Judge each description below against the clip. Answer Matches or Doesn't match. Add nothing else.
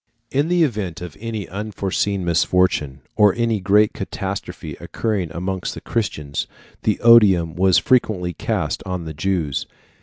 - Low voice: Matches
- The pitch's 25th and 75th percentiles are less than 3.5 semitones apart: Doesn't match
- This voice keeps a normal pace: Doesn't match